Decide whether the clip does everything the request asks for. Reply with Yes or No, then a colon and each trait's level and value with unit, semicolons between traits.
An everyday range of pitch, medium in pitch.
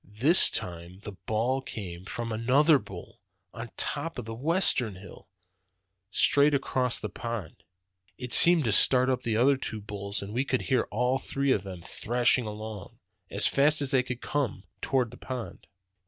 No: average, 4.2 semitones; low, 120 Hz